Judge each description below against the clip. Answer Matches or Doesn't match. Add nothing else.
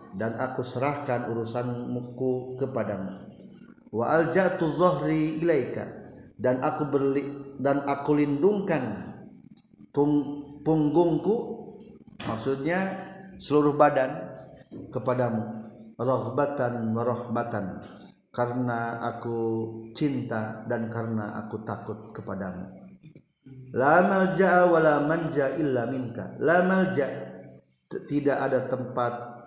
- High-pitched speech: Doesn't match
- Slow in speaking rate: Matches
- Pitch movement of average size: Matches